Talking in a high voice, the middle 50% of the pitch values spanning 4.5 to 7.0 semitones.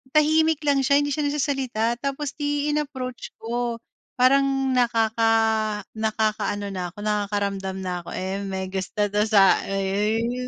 Yes: high, 230 Hz; average, 5.3 semitones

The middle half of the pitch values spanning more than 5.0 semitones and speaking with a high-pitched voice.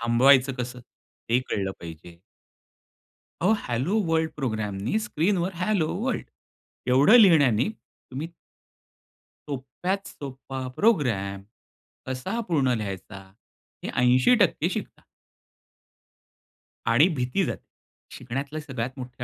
No: wide, 5.6 semitones; low, 130 Hz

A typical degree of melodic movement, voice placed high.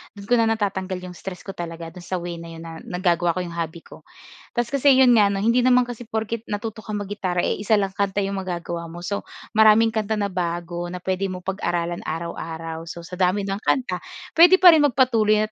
Yes: average, 3.9 semitones; high, 195 Hz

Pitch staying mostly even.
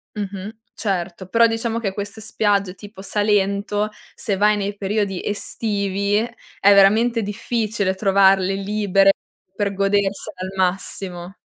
Yes: narrow, 1.5 semitones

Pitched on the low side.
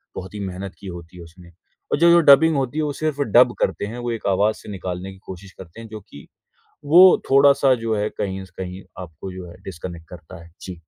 Yes: very low, 95 Hz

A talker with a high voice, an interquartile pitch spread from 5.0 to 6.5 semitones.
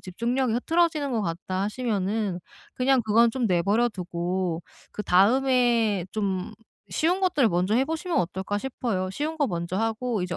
Yes: high, 220 Hz; wide, 5.5 semitones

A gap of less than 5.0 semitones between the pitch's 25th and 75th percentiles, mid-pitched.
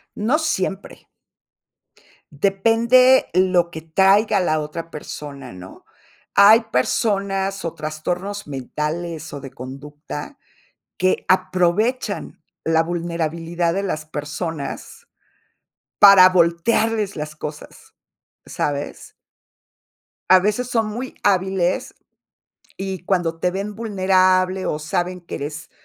Yes: average, 4.2 semitones; medium, 180 Hz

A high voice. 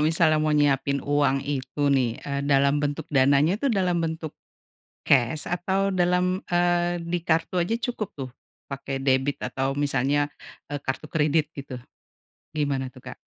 No: medium, 145 Hz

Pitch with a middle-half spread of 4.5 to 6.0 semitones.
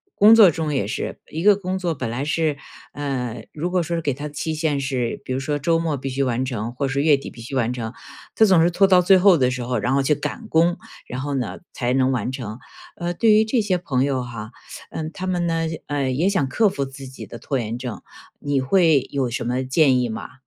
Yes: average, 4.8 semitones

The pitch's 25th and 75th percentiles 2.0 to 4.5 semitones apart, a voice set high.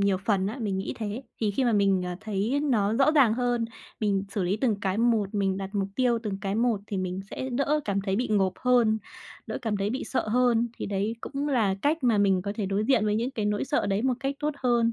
Yes: average, 3.8 semitones; high, 215 Hz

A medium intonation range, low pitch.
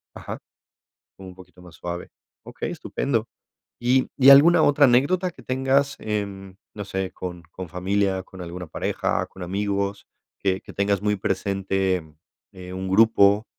Yes: average, 3.5 semitones; low, 100 Hz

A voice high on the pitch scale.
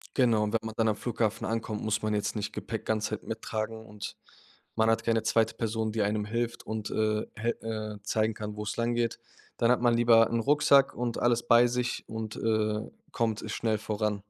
No: low, 110 Hz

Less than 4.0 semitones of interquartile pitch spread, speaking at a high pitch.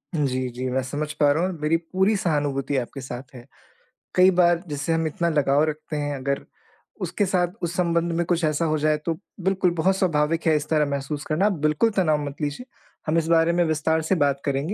No: average, 2.9 semitones; medium, 155 Hz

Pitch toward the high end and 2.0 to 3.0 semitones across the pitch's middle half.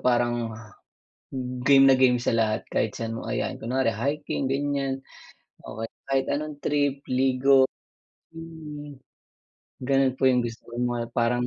No: low, 130 Hz; average, 2.7 semitones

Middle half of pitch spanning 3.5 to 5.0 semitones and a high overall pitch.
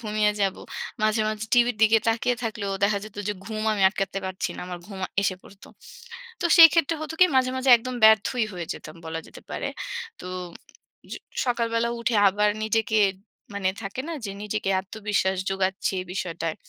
No: average, 3.0 semitones; high, 210 Hz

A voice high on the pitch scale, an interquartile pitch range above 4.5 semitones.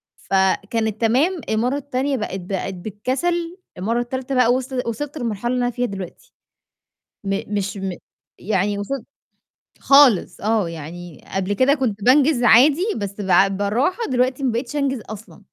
Yes: high, 230 Hz; average, 4.9 semitones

